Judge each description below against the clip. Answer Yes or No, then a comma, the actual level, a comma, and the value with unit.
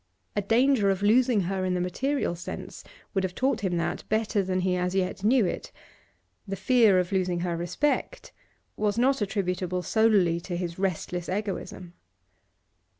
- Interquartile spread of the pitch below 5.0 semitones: Yes, average, 3.3 semitones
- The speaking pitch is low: No, high, 190 Hz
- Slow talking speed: No, average, 160 wpm